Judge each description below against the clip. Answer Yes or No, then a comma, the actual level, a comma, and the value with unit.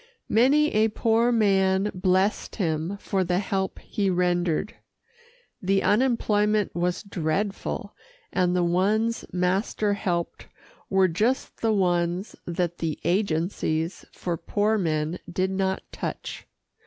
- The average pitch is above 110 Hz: Yes, high, 190 Hz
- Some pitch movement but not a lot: Yes, average, 3.1 semitones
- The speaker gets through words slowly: Yes, slow, 115 wpm